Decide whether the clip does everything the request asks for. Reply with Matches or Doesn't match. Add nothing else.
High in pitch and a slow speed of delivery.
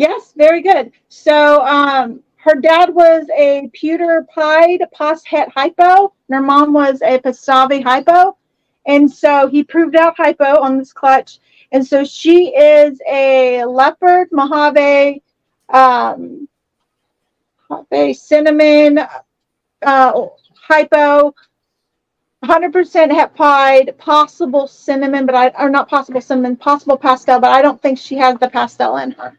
Matches